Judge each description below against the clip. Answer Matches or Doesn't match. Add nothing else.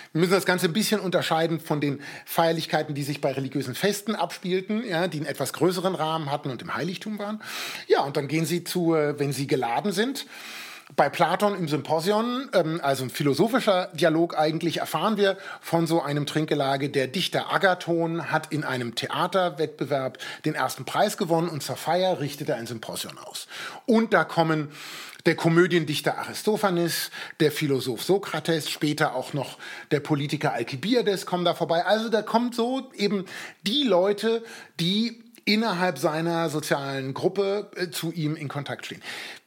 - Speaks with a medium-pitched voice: Matches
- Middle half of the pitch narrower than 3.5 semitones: Doesn't match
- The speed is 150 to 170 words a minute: Matches